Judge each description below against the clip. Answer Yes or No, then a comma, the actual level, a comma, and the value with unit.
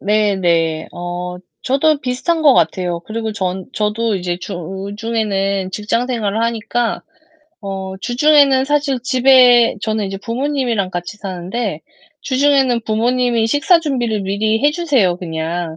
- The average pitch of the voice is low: No, high, 220 Hz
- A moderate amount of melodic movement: Yes, average, 5.0 semitones